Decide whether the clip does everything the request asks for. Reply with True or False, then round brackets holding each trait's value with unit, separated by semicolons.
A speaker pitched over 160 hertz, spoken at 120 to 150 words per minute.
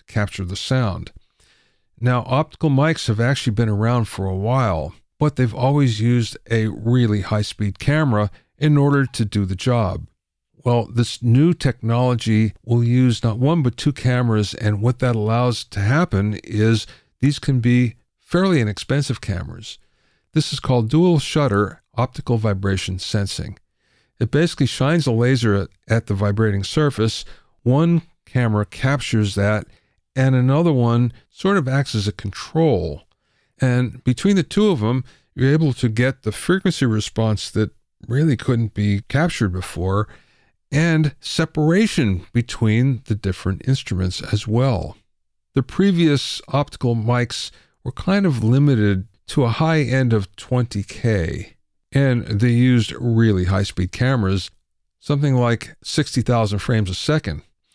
False (120 Hz; 140 wpm)